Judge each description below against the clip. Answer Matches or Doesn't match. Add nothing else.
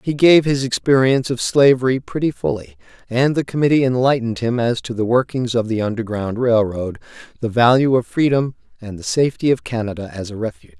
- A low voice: Matches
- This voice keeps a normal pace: Matches